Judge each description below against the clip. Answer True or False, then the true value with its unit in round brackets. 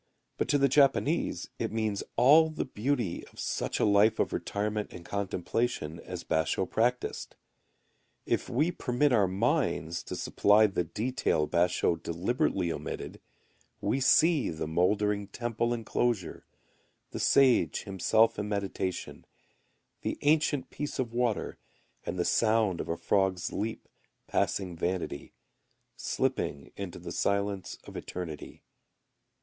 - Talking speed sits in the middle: False (130 wpm)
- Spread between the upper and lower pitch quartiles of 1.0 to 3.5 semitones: False (5.2 semitones)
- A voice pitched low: True (105 Hz)